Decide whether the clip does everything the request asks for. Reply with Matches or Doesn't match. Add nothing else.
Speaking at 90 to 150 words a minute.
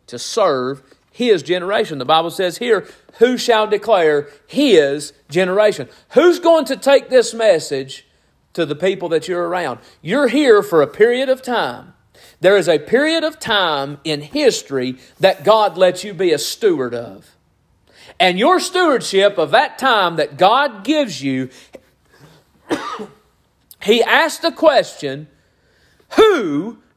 Matches